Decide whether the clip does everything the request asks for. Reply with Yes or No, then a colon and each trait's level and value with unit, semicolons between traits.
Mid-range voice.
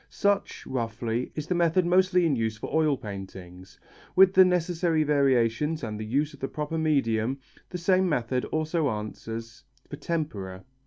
Yes: medium, 145 Hz